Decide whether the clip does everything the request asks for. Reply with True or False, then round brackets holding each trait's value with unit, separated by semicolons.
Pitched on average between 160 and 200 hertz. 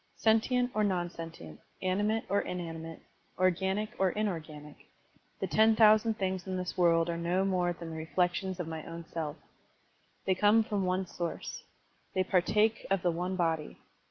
True (185 Hz)